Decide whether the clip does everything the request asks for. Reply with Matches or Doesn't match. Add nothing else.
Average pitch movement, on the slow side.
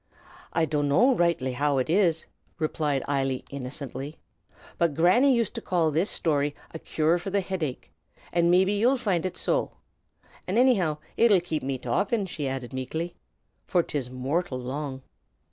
Doesn't match